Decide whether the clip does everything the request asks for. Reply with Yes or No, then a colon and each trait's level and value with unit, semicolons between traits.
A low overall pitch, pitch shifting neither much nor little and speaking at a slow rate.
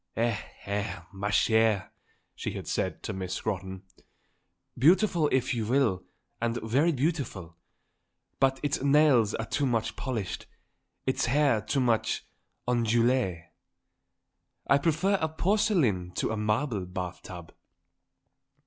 No: low, 120 Hz; wide, 5.7 semitones; slow, 120 wpm